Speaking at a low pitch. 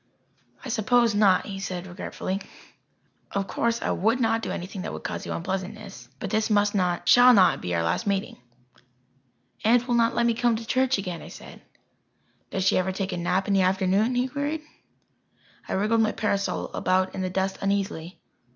No: high, 200 Hz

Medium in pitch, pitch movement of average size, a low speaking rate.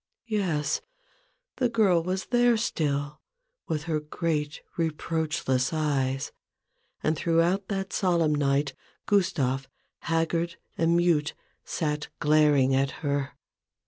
Yes: medium, 155 Hz; average, 3.1 semitones; slow, 105 wpm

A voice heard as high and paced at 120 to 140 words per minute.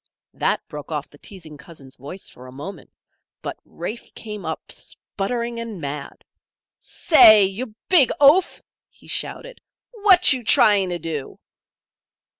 Yes: high, 195 Hz; slow, 135 wpm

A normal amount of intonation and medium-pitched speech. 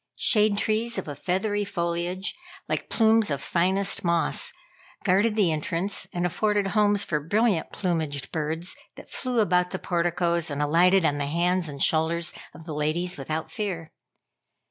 Yes: average, 3.9 semitones; medium, 175 Hz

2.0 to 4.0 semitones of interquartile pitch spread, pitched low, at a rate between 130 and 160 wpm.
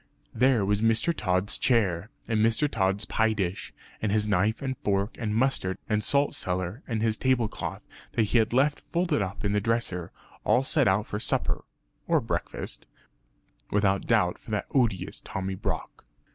No: average, 3.3 semitones; low, 110 Hz; average, 170 wpm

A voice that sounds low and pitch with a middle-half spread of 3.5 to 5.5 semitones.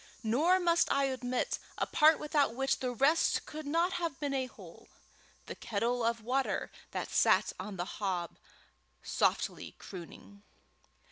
No: very high, 265 Hz; average, 5.1 semitones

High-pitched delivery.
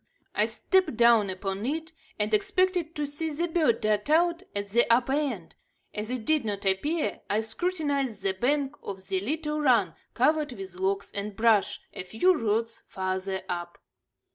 Yes: high, 230 Hz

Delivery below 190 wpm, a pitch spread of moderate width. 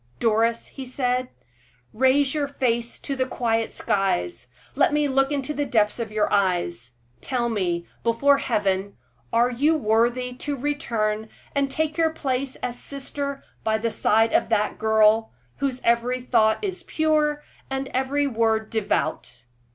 Yes: average, 150 wpm; average, 4.1 semitones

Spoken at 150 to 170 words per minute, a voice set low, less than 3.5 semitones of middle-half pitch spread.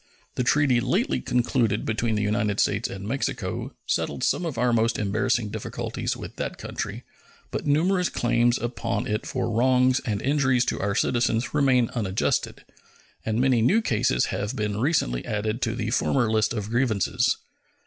Yes: average, 160 wpm; low, 120 Hz; average, 3.1 semitones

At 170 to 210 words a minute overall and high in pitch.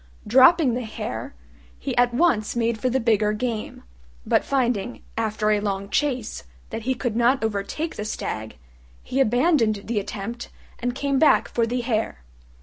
No: average, 160 wpm; high, 235 Hz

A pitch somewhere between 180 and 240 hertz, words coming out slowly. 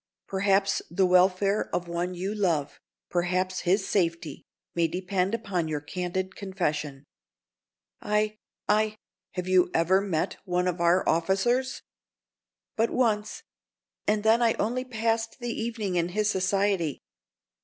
Yes: high, 190 Hz; slow, 125 wpm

